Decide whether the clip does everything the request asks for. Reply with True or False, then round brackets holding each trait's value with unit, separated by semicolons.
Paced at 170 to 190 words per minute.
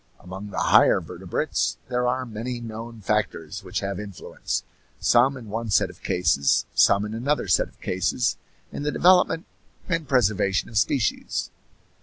False (155 wpm)